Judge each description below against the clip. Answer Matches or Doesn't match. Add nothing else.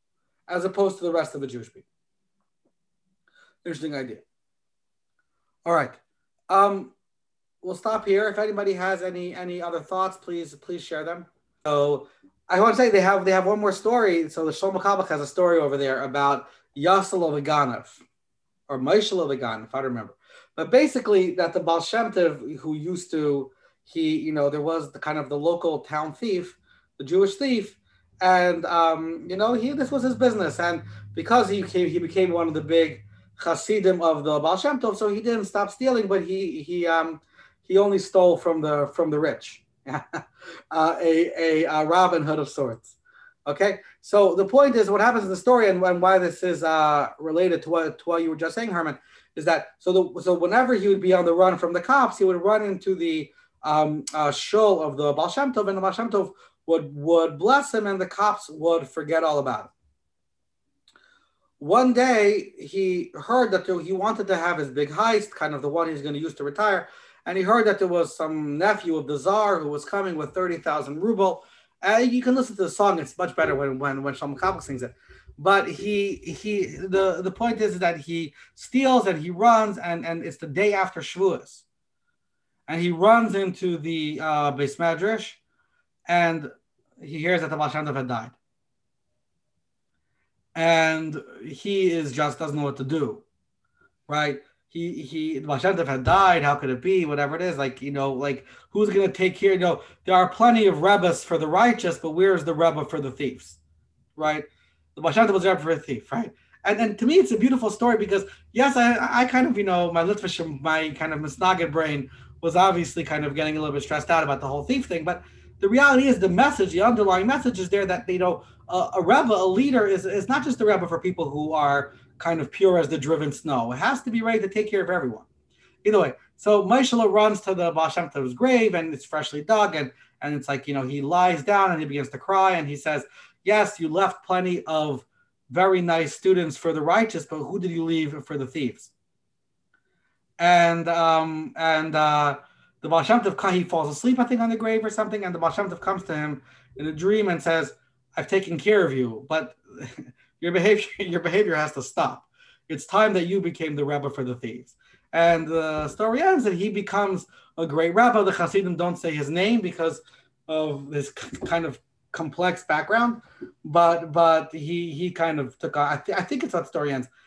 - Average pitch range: Matches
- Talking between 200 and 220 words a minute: Matches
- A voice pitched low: Doesn't match